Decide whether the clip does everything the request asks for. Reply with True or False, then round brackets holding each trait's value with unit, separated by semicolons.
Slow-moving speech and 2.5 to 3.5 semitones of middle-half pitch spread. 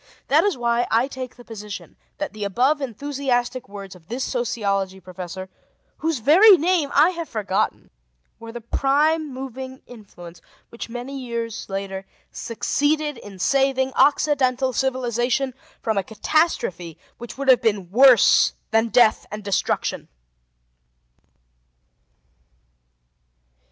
False (120 wpm; 4.6 semitones)